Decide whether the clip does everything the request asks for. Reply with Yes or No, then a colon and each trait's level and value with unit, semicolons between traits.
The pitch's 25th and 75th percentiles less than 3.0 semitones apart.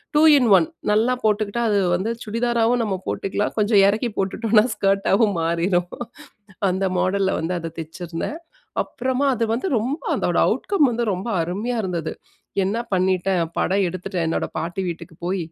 No: average, 4.1 semitones